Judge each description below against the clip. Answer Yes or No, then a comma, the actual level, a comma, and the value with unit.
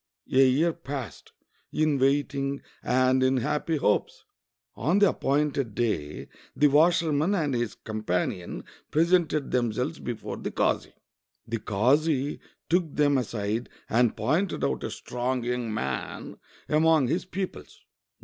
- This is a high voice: No, low, 135 Hz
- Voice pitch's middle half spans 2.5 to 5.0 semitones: Yes, average, 4.4 semitones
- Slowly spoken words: Yes, slow, 125 wpm